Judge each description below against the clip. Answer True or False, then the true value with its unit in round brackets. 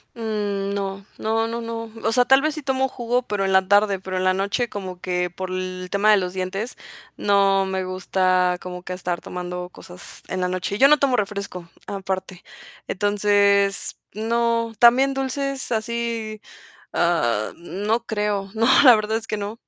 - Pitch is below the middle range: False (200 Hz)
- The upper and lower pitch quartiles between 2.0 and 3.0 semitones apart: False (3.6 semitones)